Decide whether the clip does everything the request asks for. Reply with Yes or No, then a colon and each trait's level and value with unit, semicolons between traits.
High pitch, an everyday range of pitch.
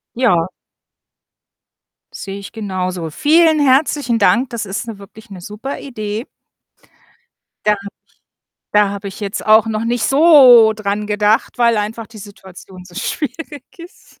Yes: high, 215 Hz; average, 3.6 semitones